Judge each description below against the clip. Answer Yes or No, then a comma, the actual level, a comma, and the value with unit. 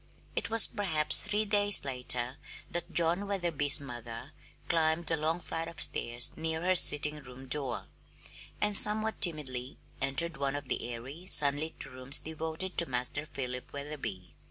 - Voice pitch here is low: No, medium, 150 Hz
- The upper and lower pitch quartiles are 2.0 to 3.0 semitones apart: No, average, 4.4 semitones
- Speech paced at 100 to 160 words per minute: Yes, average, 150 wpm